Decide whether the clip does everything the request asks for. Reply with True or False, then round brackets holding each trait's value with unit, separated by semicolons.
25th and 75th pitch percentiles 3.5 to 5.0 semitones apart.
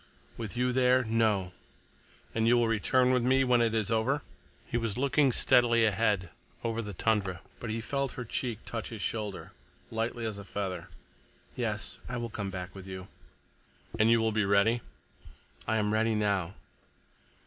False (2.8 semitones)